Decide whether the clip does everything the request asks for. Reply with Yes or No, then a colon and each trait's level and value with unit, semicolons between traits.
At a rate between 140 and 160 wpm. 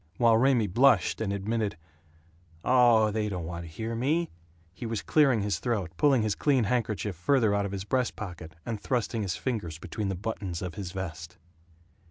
No: average, 185 wpm